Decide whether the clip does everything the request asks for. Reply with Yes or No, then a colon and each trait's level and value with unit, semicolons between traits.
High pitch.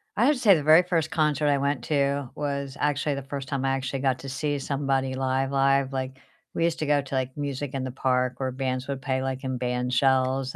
No: low, 135 Hz